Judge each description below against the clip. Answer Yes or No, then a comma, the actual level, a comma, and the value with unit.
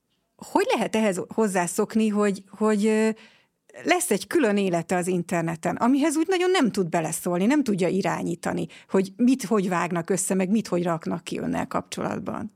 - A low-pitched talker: No, high, 205 Hz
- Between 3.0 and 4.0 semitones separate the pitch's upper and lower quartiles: Yes, average, 3.7 semitones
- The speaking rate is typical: No, fast, 160 wpm